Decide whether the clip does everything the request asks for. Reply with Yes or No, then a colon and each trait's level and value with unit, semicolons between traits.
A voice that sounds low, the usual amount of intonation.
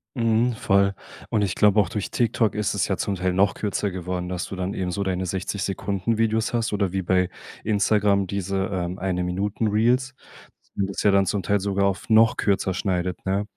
No: low, 100 Hz; narrow, 2.2 semitones